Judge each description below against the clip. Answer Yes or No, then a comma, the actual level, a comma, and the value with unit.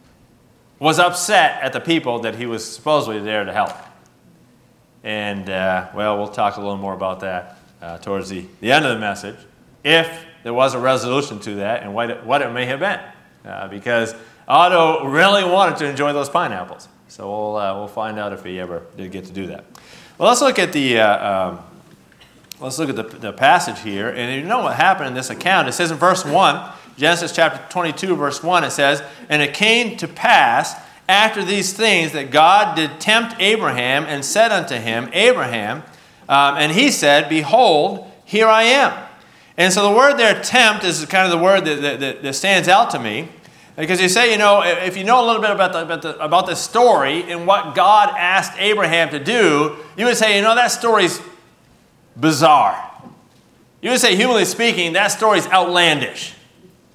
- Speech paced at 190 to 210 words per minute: Yes, average, 200 wpm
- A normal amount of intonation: No, wide, 8.1 semitones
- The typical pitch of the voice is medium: Yes, medium, 160 Hz